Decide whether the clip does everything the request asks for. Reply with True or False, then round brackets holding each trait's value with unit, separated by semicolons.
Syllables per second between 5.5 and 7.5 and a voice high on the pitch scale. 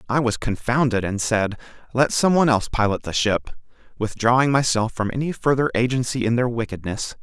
False (5.6 syllables/s; 120 Hz)